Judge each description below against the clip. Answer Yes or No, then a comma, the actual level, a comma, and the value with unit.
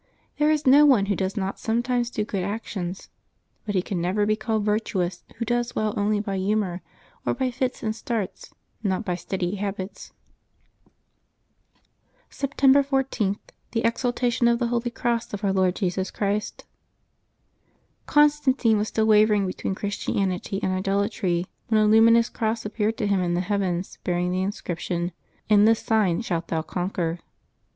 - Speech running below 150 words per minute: No, average, 160 wpm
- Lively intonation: No, average, 3.6 semitones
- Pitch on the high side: Yes, high, 210 Hz